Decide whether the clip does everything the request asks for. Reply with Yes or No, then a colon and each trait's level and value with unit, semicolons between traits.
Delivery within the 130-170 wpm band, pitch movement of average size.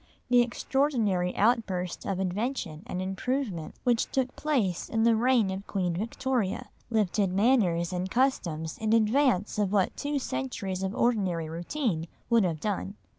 Yes: average, 145 wpm; average, 5.0 semitones